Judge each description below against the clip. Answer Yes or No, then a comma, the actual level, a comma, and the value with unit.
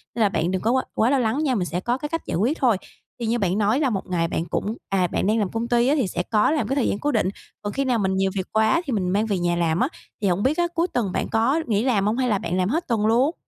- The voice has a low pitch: No, high, 220 Hz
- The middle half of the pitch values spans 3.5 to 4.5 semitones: No, average, 5.2 semitones